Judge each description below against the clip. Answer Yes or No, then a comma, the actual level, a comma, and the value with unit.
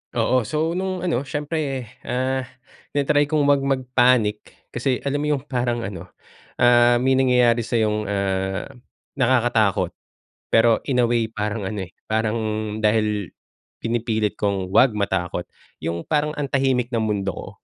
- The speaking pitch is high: No, low, 120 Hz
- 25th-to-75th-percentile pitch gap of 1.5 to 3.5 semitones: No, average, 4.2 semitones